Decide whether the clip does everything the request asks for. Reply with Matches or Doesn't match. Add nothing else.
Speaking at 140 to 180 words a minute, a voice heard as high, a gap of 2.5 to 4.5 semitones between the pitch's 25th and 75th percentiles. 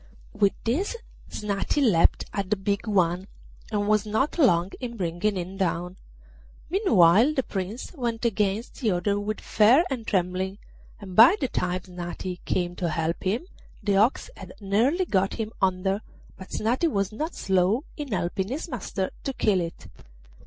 Matches